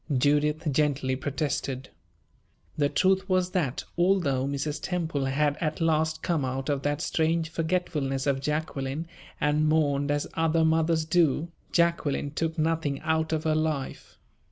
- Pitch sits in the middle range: Yes, medium, 155 Hz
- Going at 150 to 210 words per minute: No, average, 140 wpm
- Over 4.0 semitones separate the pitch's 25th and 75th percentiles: No, narrow, 2.4 semitones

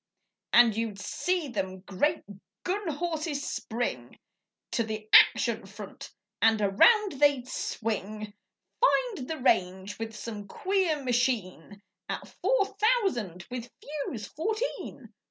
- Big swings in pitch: Yes, wide, 7.8 semitones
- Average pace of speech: No, slow, 115 wpm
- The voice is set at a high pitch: Yes, high, 245 Hz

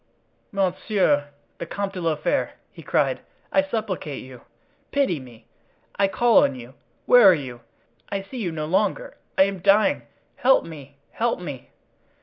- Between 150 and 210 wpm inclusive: No, average, 140 wpm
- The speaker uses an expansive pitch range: Yes, wide, 6.3 semitones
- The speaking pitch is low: No, medium, 185 Hz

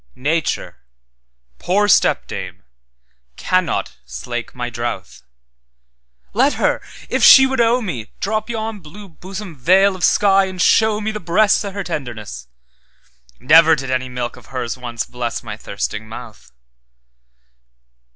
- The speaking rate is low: Yes, slow, 115 wpm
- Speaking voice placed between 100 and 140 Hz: Yes, low, 135 Hz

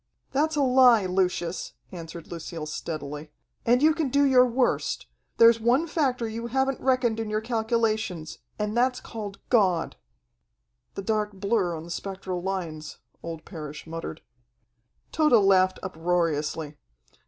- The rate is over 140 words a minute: No, slow, 135 wpm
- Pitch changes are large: Yes, wide, 6.4 semitones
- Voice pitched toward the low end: No, high, 210 Hz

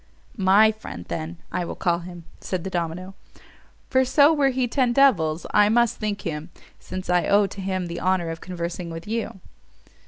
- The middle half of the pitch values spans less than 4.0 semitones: No, average, 4.3 semitones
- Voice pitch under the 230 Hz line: Yes, medium, 185 Hz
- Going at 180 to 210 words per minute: Yes, average, 185 wpm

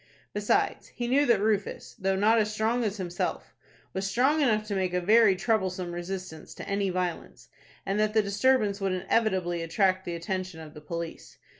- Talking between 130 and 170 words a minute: No, average, 180 wpm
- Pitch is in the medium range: No, high, 195 Hz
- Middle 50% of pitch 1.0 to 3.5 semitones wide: Yes, average, 3.1 semitones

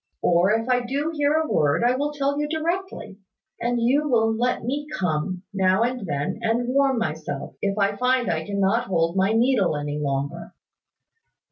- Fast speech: No, average, 175 wpm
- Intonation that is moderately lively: No, wide, 6.4 semitones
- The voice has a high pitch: Yes, high, 225 Hz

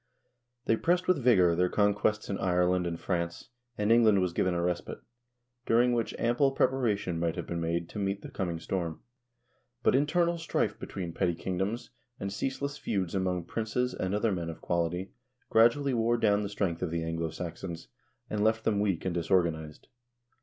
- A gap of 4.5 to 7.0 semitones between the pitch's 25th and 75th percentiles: Yes, average, 4.8 semitones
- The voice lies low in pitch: Yes, very low, 95 Hz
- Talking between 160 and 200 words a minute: Yes, average, 175 wpm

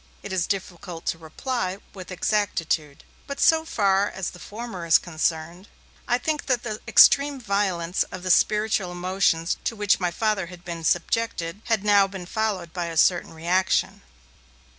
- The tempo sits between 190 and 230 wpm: No, average, 160 wpm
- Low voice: No, high, 190 Hz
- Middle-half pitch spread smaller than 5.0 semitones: Yes, average, 3.8 semitones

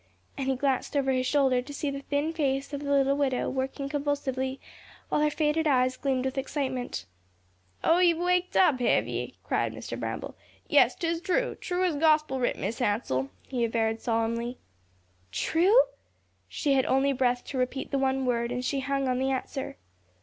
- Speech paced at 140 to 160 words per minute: No, average, 180 wpm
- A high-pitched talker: Yes, very high, 270 Hz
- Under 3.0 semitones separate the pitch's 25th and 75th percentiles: Yes, narrow, 2.5 semitones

